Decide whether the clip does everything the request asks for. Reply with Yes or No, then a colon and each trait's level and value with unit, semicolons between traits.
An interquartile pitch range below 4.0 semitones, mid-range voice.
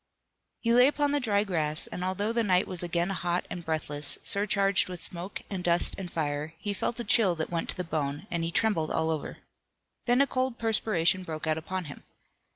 No: average, 4.4 semitones; medium, 180 Hz